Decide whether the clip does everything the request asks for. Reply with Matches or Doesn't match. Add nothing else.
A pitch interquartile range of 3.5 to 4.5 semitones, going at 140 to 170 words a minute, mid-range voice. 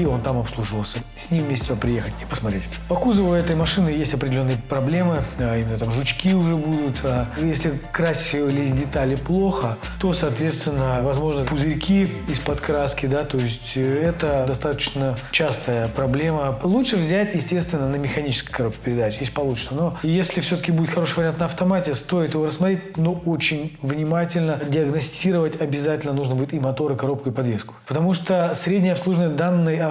Matches